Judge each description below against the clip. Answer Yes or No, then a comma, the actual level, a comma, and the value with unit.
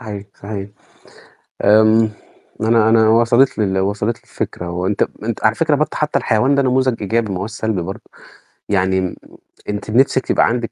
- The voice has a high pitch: No, low, 110 Hz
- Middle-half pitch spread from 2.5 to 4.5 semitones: Yes, average, 2.9 semitones